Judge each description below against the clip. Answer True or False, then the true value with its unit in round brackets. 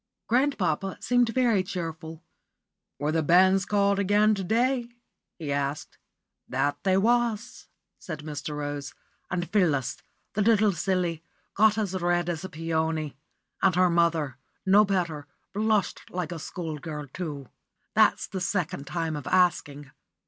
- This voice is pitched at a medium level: True (175 Hz)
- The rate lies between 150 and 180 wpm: False (140 wpm)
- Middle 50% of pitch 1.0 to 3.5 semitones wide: False (4.3 semitones)